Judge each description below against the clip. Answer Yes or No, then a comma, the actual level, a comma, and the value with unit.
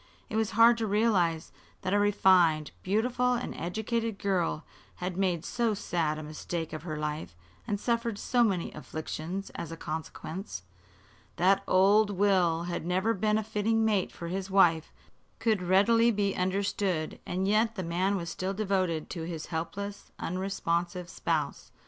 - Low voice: No, high, 190 Hz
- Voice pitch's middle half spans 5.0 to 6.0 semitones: No, average, 3.7 semitones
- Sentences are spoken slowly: No, average, 155 wpm